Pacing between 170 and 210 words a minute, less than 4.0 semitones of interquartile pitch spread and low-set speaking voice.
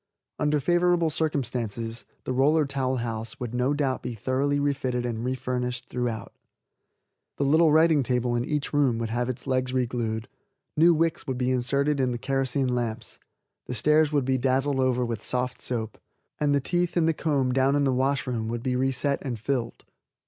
Yes: average, 185 wpm; average, 2.7 semitones; low, 130 Hz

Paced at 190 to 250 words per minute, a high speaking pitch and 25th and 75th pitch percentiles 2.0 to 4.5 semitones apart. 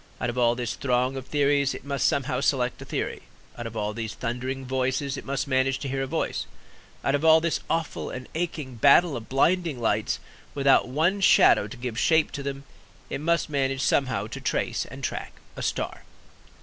No: average, 200 wpm; low, 135 Hz; narrow, 2.5 semitones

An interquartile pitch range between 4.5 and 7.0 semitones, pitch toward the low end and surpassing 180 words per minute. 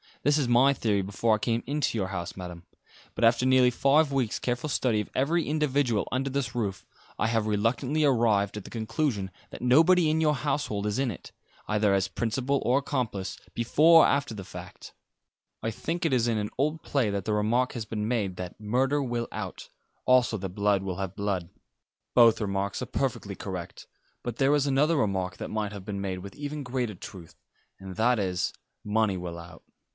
Yes: average, 5.2 semitones; low, 115 Hz; average, 195 wpm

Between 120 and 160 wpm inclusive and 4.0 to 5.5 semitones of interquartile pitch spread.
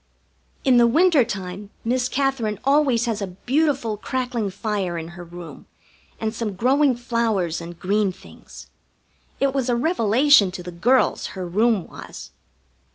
Yes: average, 150 wpm; average, 5.2 semitones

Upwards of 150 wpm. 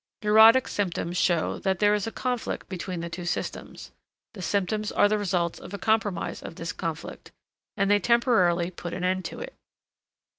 Yes: average, 180 wpm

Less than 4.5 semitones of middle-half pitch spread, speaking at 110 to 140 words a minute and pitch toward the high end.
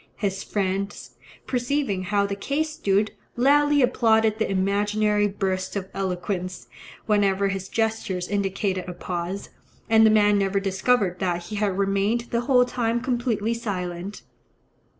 Yes: average, 2.8 semitones; slow, 135 wpm; high, 205 Hz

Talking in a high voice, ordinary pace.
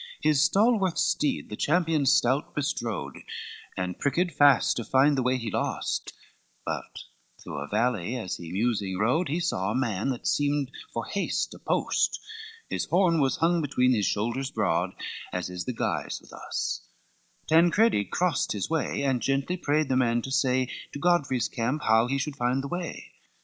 No: low, 135 Hz; average, 175 wpm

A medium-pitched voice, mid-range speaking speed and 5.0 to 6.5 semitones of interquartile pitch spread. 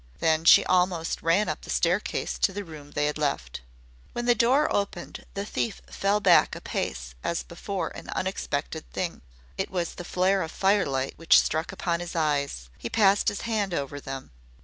Yes: medium, 170 Hz; average, 185 wpm; wide, 5.6 semitones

